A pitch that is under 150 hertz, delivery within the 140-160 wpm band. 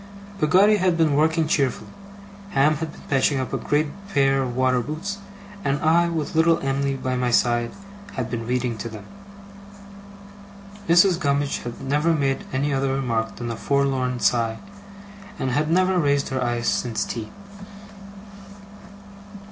Yes: low, 135 Hz; average, 150 wpm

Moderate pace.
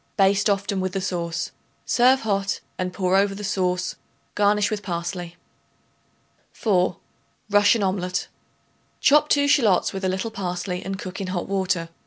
Yes: average, 150 wpm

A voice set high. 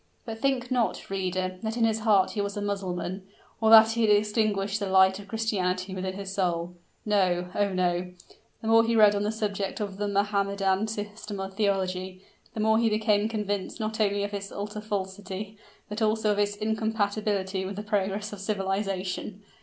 Yes: high, 205 Hz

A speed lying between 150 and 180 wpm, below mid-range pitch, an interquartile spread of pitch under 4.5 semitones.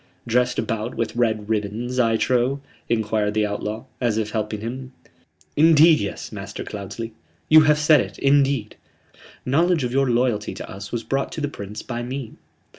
Yes: average, 170 wpm; low, 120 Hz; average, 4.0 semitones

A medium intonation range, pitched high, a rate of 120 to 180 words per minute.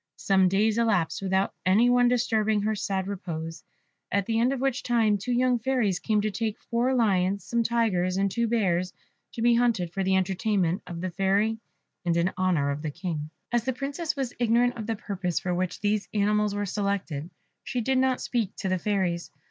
No: average, 4.1 semitones; high, 205 Hz; average, 200 wpm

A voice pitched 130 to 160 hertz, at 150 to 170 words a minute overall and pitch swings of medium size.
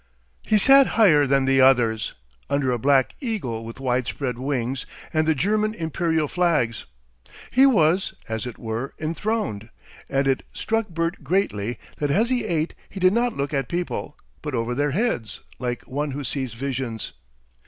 No: medium, 140 Hz; average, 165 wpm; wide, 6.4 semitones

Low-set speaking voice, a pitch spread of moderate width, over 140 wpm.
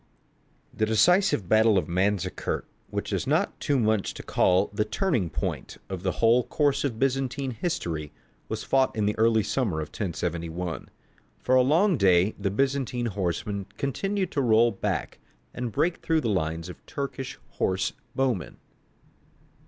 No: low, 110 Hz; wide, 6.2 semitones; average, 160 wpm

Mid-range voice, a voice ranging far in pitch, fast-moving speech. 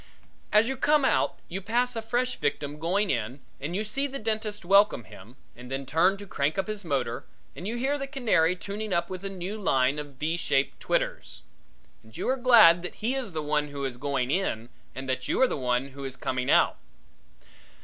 Yes: medium, 175 Hz; wide, 7.8 semitones; fast, 215 wpm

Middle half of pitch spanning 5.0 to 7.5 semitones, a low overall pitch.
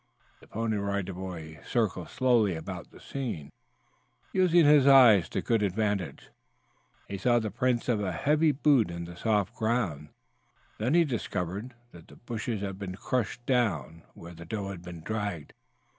Yes: wide, 5.5 semitones; low, 105 Hz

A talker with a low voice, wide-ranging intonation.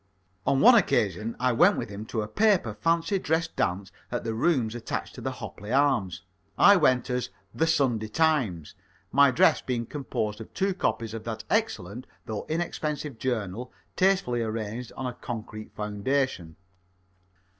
Yes: low, 125 Hz; wide, 6.1 semitones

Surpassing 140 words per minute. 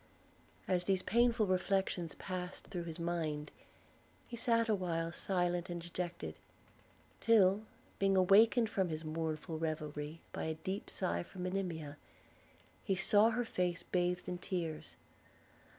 No: slow, 135 wpm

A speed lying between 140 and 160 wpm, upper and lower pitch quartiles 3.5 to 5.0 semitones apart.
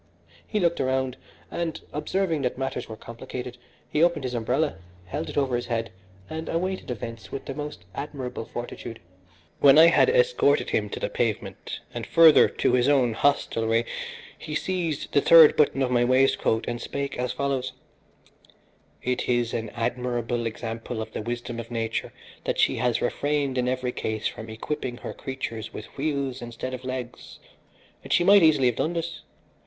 No: average, 170 wpm; average, 3.9 semitones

